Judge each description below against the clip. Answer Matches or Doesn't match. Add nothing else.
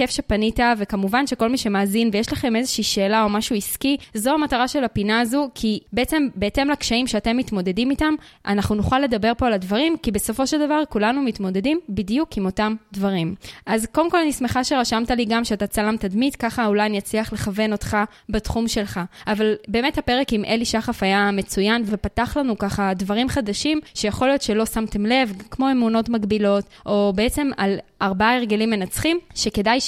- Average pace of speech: Doesn't match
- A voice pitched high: Matches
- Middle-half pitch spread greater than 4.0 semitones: Doesn't match